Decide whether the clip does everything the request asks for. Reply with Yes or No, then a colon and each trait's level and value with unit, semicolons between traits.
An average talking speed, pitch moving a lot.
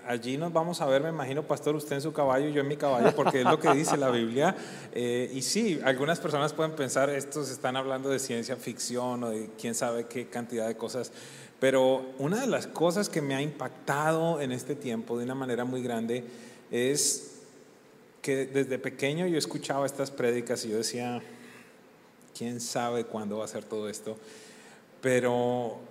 No: average, 190 wpm; average, 3.0 semitones